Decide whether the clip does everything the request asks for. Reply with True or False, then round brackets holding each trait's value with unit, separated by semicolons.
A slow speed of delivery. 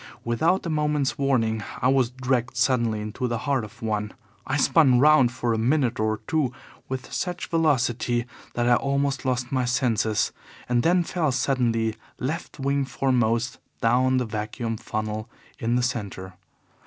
False (155 wpm)